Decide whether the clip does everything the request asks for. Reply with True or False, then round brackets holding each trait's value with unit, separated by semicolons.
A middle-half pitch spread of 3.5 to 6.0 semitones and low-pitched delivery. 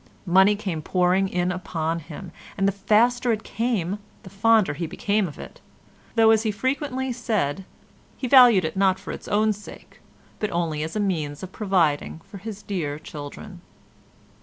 False (4.2 semitones; 195 Hz)